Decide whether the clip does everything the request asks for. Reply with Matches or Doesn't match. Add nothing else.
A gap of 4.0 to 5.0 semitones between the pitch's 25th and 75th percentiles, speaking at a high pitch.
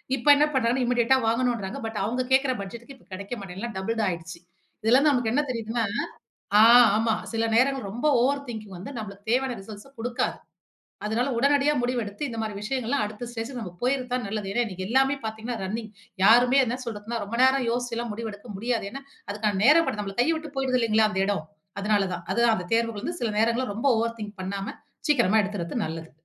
Doesn't match